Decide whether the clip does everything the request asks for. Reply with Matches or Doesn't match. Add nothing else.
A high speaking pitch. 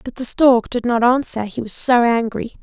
Matches